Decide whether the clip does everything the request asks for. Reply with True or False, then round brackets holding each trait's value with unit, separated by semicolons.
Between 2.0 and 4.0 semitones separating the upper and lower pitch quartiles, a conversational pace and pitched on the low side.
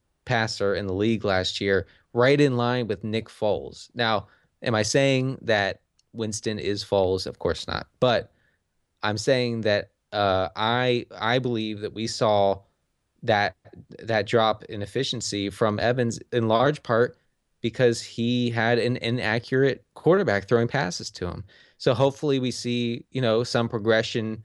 True (3.0 semitones; 150 wpm; 115 Hz)